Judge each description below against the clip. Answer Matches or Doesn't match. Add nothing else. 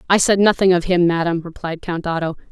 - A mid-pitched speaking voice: Matches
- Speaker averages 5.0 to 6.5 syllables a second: Matches